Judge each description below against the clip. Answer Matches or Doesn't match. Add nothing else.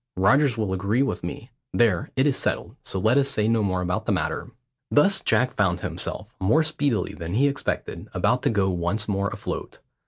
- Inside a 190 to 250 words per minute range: Matches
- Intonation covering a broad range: Matches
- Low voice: Matches